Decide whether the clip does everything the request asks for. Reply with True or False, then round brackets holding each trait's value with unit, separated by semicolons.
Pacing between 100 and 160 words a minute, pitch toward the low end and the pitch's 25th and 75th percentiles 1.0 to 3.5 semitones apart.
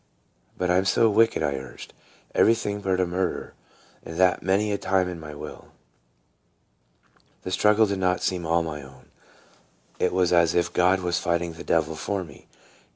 False (175 wpm; 90 Hz; 2.6 semitones)